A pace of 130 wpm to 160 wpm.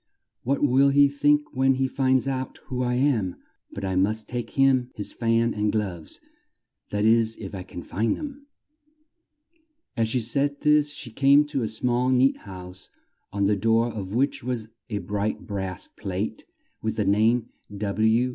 No: average, 170 wpm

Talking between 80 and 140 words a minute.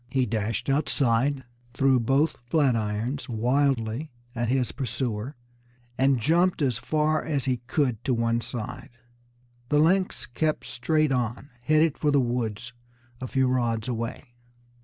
Yes: slow, 135 wpm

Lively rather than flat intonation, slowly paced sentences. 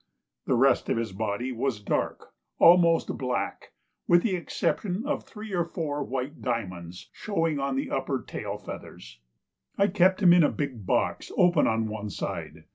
No: wide, 7.4 semitones; average, 165 wpm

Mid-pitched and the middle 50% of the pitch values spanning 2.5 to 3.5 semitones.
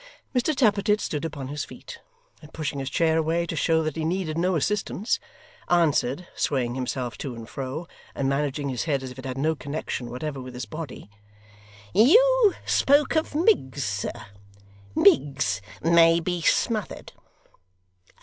No: medium, 155 Hz; average, 4.9 semitones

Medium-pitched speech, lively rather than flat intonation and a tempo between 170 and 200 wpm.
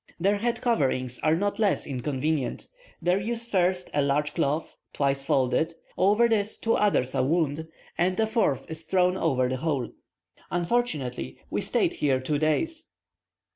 No: medium, 160 Hz; wide, 6.6 semitones; average, 155 wpm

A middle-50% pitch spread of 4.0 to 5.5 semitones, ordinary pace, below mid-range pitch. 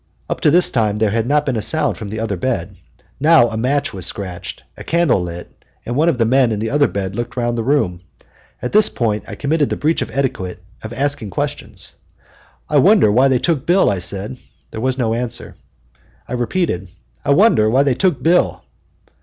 No: average, 5.1 semitones; fast, 210 wpm; low, 120 Hz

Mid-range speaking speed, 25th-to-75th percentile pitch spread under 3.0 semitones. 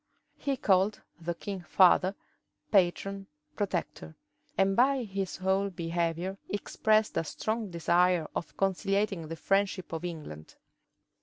No: slow, 120 wpm; narrow, 2.6 semitones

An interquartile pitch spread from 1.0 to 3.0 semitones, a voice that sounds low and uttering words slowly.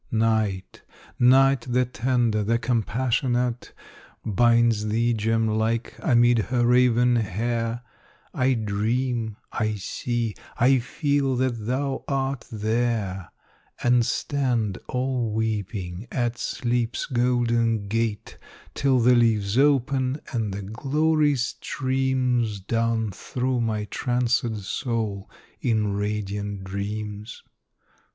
Yes: average, 2.7 semitones; low, 115 Hz; slow, 100 wpm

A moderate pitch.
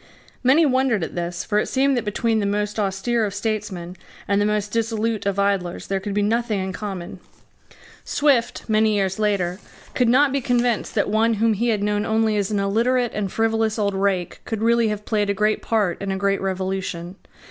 No: high, 210 Hz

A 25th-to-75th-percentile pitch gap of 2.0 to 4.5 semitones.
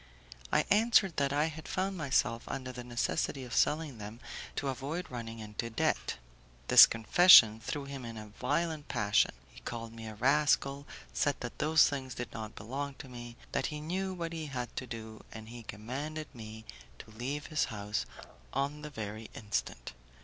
No: average, 4.9 semitones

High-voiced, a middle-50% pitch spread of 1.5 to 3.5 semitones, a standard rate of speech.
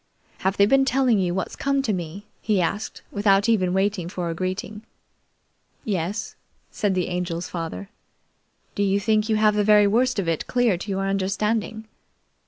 Yes: high, 200 Hz; average, 2.7 semitones; average, 175 wpm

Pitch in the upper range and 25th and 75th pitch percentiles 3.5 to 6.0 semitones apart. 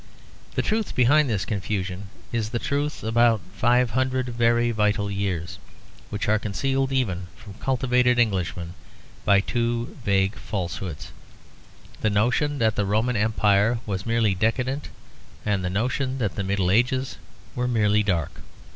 No: low, 110 Hz; average, 3.8 semitones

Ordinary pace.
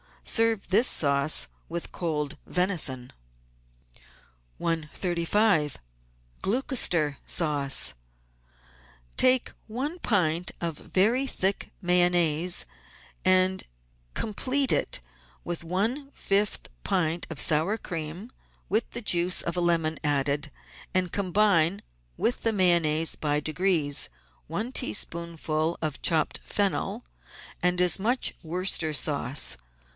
No: slow, 100 wpm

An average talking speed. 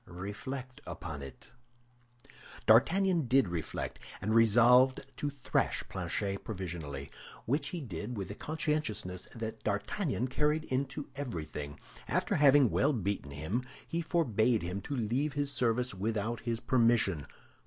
No: slow, 130 wpm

